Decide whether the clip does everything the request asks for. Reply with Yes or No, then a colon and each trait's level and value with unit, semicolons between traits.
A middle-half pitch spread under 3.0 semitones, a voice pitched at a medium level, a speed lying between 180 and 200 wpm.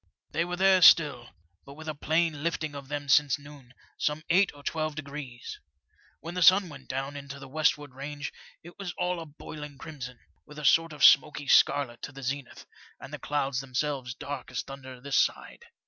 Yes: narrow, 2.4 semitones; medium, 145 Hz; average, 195 wpm